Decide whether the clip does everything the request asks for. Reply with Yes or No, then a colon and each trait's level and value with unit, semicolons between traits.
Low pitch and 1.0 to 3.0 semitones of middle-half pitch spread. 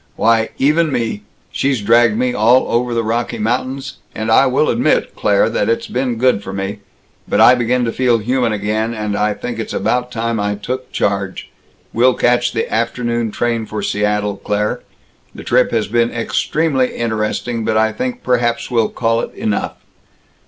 Yes: low, 115 Hz; narrow, 2.4 semitones